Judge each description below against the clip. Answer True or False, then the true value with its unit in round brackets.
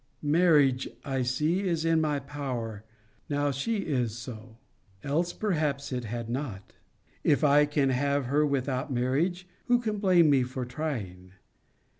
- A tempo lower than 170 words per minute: True (145 wpm)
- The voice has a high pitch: False (140 Hz)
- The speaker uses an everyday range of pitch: True (3.8 semitones)